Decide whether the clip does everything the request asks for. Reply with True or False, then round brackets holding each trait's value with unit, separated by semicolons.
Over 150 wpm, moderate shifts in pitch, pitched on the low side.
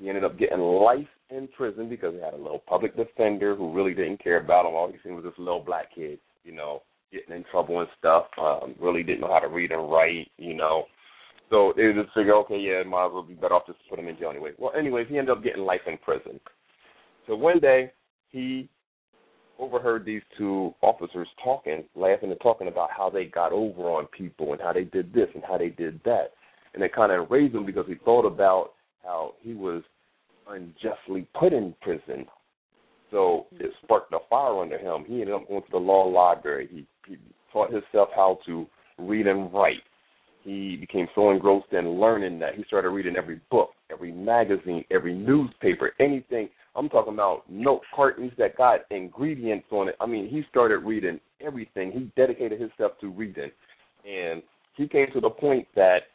False (200 wpm; 6.6 semitones; 100 Hz)